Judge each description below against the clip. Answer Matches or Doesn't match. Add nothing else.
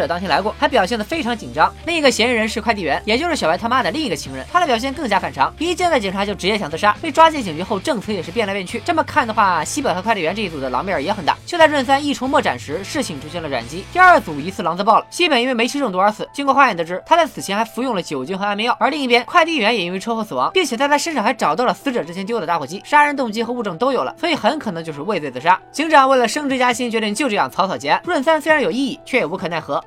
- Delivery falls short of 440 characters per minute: Doesn't match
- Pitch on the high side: Matches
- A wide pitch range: Matches